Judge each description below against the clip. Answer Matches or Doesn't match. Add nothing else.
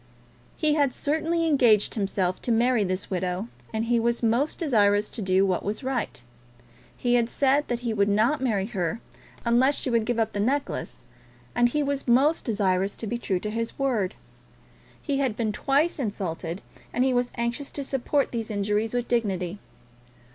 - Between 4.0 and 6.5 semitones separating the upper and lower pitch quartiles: Matches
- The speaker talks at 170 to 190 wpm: Matches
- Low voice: Doesn't match